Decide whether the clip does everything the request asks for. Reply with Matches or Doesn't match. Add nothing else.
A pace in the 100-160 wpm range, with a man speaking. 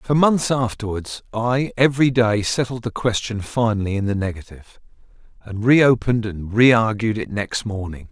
Matches